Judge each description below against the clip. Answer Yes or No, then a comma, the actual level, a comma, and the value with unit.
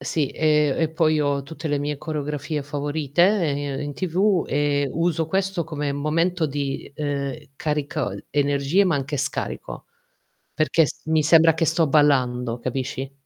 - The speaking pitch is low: No, medium, 150 Hz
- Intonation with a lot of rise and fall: No, narrow, 2.4 semitones